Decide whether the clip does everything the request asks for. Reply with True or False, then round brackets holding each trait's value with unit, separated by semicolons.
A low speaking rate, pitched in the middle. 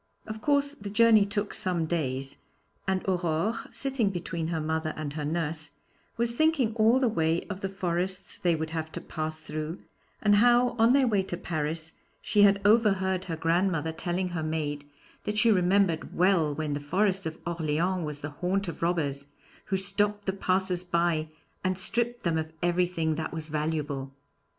False (175 wpm; 175 Hz)